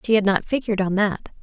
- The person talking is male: No, female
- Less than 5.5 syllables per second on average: No, 6.8 syllables/s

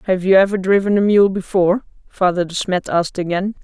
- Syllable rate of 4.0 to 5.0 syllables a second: No, 6.0 syllables/s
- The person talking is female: Yes, female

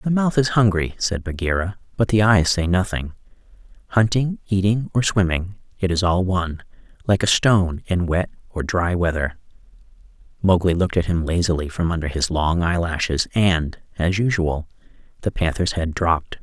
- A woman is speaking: No, male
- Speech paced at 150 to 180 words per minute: Yes, average, 155 wpm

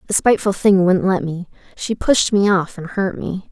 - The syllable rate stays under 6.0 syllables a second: Yes, 4.9 syllables/s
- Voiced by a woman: Yes, female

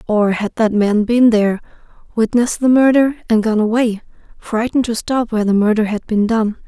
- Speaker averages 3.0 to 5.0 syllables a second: No, 5.6 syllables/s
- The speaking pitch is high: Yes, high, 225 Hz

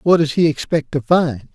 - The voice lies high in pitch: No, medium, 150 Hz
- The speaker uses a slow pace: No, fast, 235 wpm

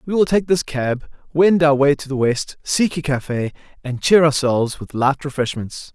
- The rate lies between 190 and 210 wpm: Yes, average, 200 wpm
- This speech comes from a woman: No, male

